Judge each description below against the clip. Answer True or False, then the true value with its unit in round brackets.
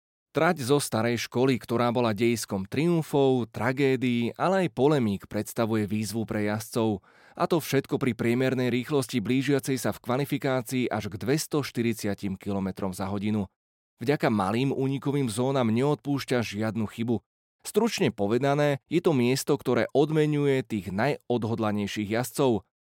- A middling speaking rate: True (130 wpm)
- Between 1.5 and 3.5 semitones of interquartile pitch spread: False (4.2 semitones)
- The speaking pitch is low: True (125 Hz)